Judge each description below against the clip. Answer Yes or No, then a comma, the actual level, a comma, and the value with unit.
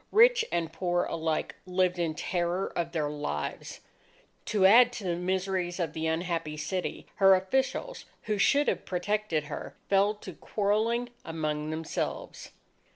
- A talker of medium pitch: Yes, medium, 180 Hz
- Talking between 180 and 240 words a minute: No, average, 145 wpm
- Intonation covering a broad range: No, average, 4.1 semitones